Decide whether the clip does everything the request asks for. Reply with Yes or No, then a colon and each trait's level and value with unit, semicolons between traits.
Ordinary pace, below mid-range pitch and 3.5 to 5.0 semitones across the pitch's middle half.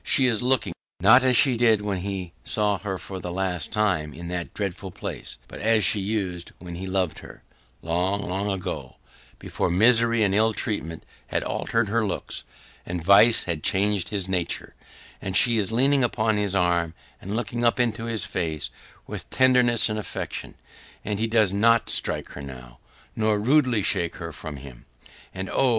Yes: average, 180 wpm; low, 100 Hz; average, 4.1 semitones